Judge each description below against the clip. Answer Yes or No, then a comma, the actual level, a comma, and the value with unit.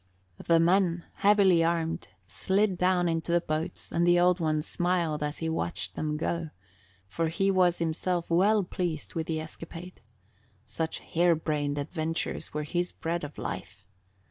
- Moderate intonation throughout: No, narrow, 2.0 semitones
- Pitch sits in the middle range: Yes, medium, 170 Hz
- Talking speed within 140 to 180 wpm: Yes, average, 150 wpm